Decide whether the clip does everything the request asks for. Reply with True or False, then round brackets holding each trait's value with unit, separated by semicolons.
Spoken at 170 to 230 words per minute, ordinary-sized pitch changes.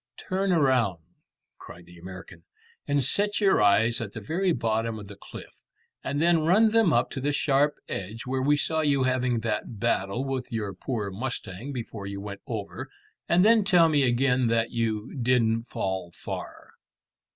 False (175 wpm; 5.7 semitones)